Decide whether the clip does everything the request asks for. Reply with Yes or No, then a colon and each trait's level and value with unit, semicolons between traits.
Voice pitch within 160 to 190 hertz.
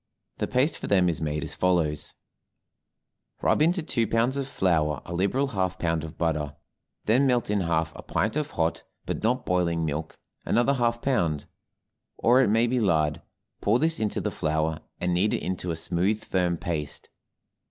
No: very low, 90 Hz